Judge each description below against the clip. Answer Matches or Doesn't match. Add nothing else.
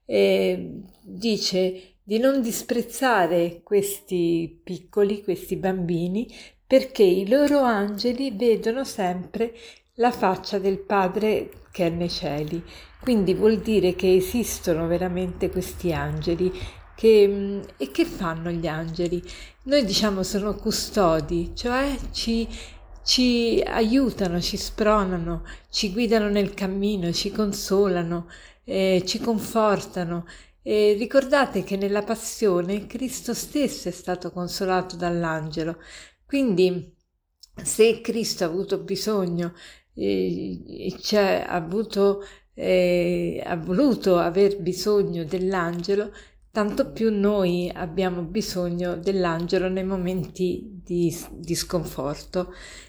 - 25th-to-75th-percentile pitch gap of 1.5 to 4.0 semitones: Matches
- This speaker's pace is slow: Matches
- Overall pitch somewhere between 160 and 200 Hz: Matches